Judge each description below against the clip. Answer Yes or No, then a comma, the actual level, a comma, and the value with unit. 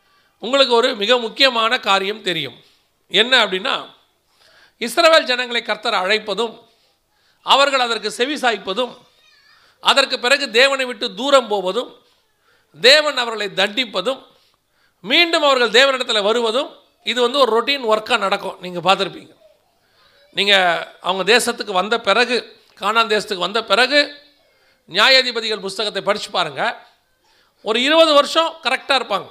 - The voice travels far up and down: No, average, 4.5 semitones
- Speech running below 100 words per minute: No, average, 110 wpm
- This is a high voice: Yes, high, 240 Hz